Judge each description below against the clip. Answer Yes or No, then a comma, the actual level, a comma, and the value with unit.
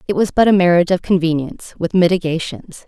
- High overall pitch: No, medium, 175 Hz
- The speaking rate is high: No, average, 190 wpm